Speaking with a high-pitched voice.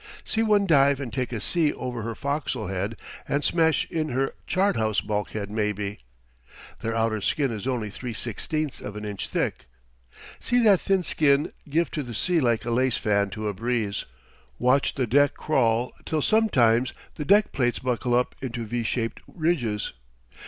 No: low, 125 Hz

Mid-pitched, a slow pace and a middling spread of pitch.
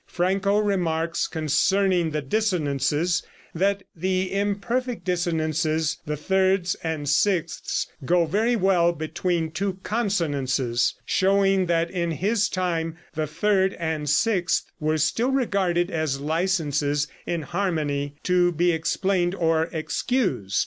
Yes: medium, 175 Hz; slow, 115 wpm; average, 3.5 semitones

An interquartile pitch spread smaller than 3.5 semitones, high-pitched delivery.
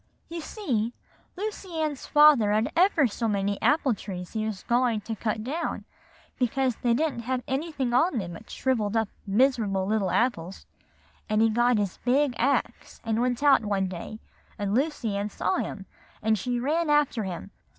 No: average, 4.8 semitones; high, 235 Hz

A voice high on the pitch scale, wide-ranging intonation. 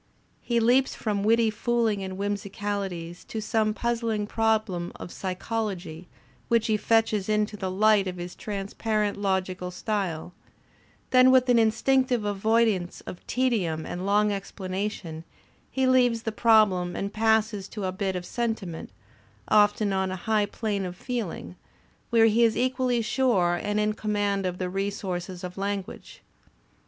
No: high, 205 Hz; average, 3.0 semitones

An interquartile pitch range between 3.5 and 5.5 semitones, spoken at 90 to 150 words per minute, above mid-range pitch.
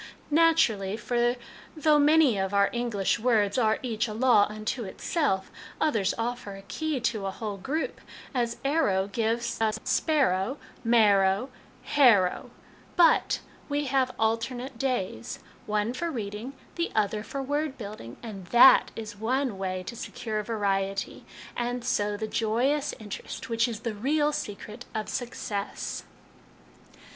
Yes: average, 4.2 semitones; average, 145 wpm; high, 230 Hz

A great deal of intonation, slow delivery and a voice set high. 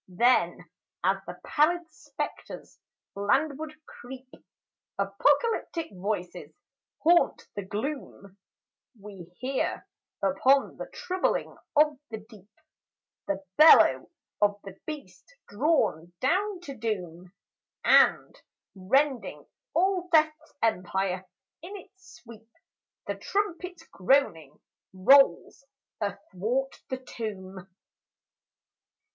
Yes: wide, 7.8 semitones; slow, 90 wpm; very high, 255 Hz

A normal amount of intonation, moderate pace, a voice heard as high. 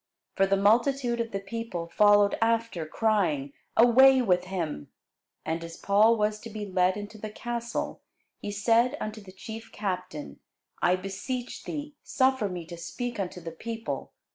Yes: average, 4.0 semitones; average, 160 wpm; high, 210 Hz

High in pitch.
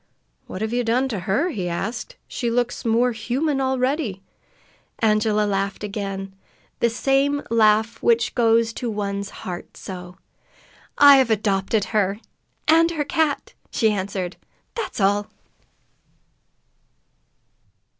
Yes: high, 225 Hz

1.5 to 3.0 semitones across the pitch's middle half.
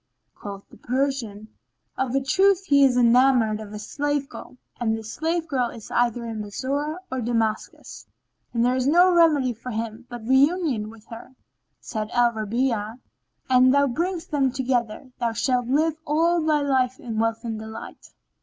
No: average, 3.8 semitones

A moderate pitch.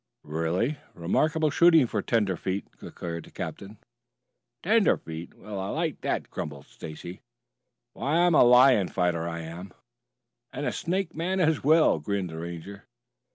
No: low, 100 Hz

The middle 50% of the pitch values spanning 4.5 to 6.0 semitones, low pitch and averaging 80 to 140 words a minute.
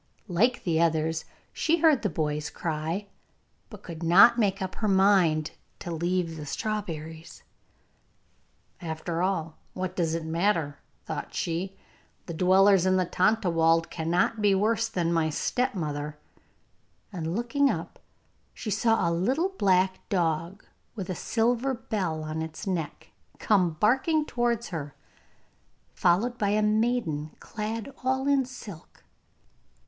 No: average, 5.1 semitones; medium, 185 Hz; slow, 135 wpm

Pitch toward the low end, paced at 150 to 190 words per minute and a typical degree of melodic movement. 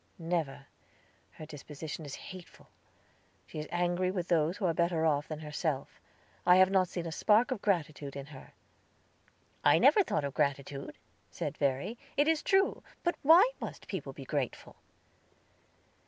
No: medium, 165 Hz; average, 155 wpm; average, 4.1 semitones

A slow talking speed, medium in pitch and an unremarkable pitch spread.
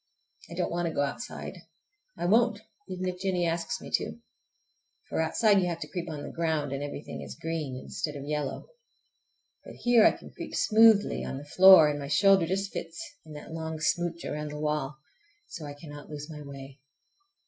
No: average, 195 wpm; medium, 160 Hz; average, 3.7 semitones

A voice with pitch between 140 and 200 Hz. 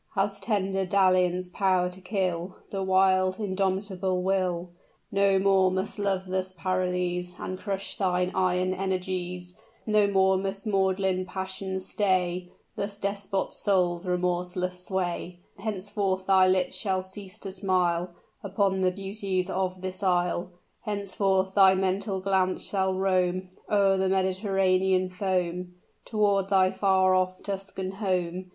Yes: high, 190 Hz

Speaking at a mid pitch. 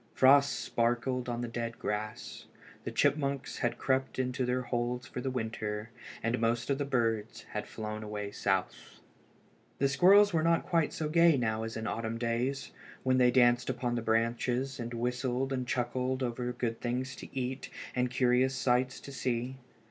No: low, 125 Hz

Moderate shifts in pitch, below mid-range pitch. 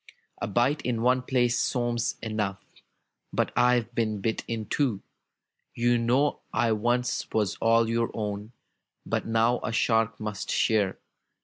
No: narrow, 1.9 semitones; low, 115 Hz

